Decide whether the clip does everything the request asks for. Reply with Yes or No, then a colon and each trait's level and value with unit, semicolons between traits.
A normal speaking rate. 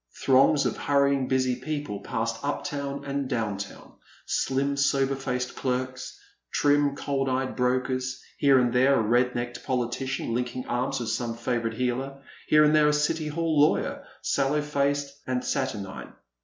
Yes: average, 155 wpm